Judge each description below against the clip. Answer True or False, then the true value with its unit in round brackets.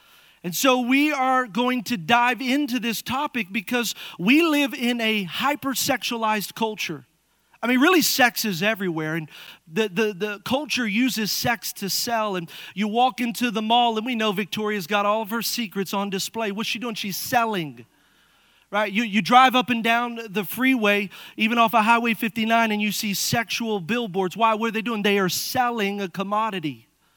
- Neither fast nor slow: True (185 wpm)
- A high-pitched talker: True (225 Hz)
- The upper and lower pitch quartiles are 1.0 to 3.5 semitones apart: True (3.0 semitones)